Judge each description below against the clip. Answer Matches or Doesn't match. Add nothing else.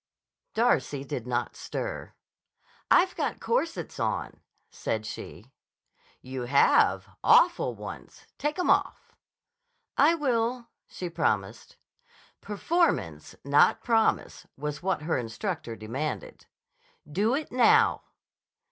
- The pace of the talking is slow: Matches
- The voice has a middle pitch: Doesn't match